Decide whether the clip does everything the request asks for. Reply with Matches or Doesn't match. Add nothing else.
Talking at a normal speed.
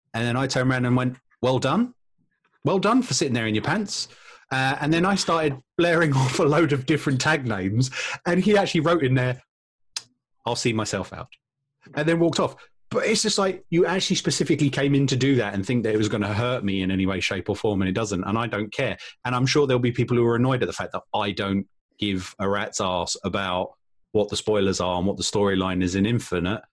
Doesn't match